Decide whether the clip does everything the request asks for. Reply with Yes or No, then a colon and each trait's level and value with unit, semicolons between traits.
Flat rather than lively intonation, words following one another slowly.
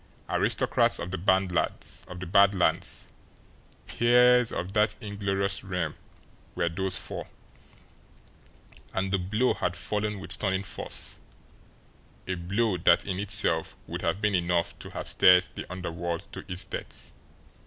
Yes: narrow, 2.3 semitones; slow, 130 wpm